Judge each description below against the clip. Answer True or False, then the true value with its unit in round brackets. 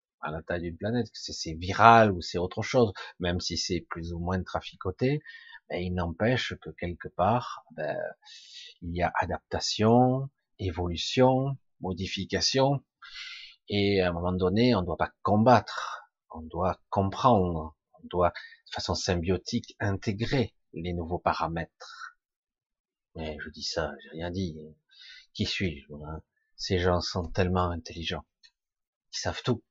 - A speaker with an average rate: False (140 wpm)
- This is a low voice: True (95 Hz)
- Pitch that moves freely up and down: False (5.0 semitones)